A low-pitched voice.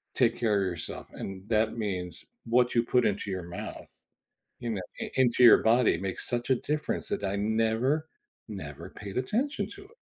Yes: low, 110 Hz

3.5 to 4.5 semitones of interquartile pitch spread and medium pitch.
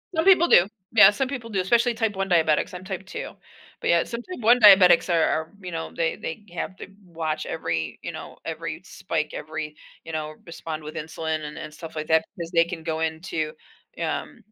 Yes: average, 3.9 semitones; medium, 165 Hz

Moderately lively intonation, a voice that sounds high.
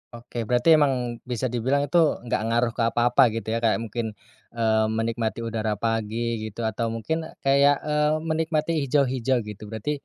No: average, 3.7 semitones; low, 120 Hz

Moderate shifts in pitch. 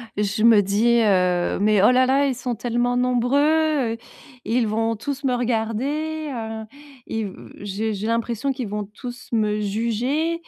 Yes: average, 3.2 semitones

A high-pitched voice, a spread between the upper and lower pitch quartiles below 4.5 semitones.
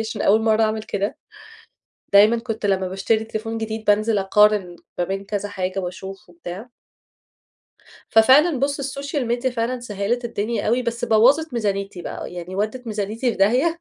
Yes: high, 220 Hz; average, 3.3 semitones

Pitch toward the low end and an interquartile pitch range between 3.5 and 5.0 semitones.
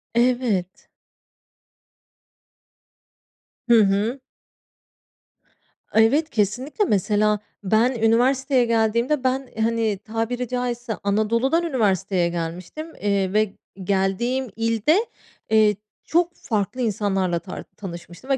No: high, 225 Hz; average, 3.9 semitones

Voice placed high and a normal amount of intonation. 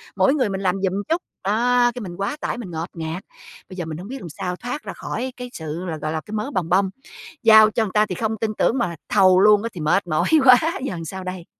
Yes: high, 195 Hz; average, 4.4 semitones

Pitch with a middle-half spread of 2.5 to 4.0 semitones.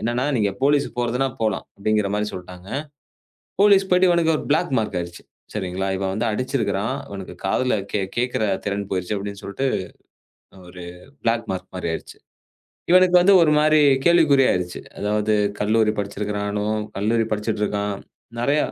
No: average, 5.1 semitones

